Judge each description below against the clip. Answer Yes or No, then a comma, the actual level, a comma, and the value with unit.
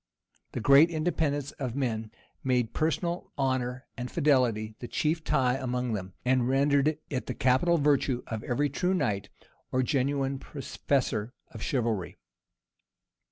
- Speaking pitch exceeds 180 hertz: No, low, 130 Hz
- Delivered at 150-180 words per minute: No, slow, 135 wpm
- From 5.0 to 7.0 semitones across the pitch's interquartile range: No, average, 2.9 semitones